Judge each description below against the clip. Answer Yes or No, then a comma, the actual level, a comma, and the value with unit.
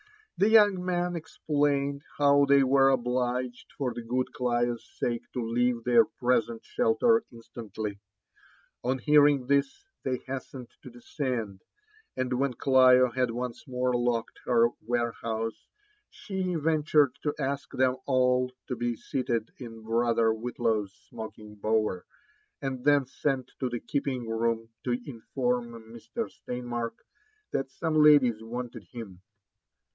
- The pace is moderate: No, slow, 130 wpm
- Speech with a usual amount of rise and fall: Yes, average, 3.0 semitones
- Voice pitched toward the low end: Yes, low, 125 Hz